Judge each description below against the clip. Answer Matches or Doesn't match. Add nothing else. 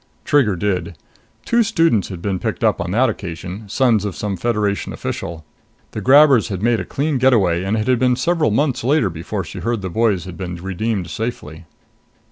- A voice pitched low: Matches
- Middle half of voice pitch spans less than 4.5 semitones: Doesn't match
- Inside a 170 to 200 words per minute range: Matches